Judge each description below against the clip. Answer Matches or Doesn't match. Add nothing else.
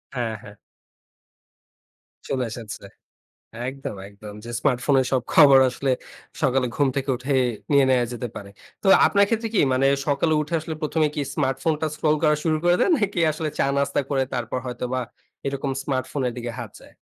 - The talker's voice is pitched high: Doesn't match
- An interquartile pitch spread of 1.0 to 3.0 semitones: Doesn't match